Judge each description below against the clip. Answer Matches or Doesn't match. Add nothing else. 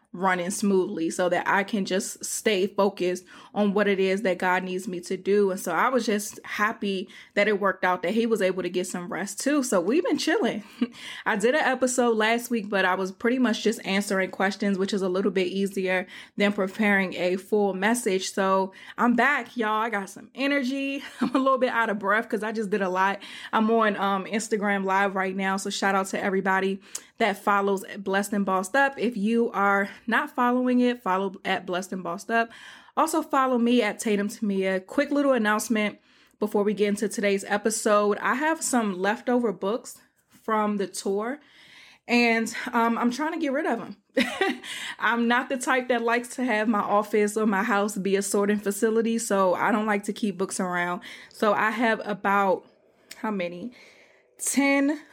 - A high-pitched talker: Matches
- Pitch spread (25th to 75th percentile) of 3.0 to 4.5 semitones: Matches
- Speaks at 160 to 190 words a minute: Doesn't match